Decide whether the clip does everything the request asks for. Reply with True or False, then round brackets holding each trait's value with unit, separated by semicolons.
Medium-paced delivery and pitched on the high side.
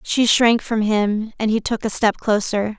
False (215 wpm; 220 Hz)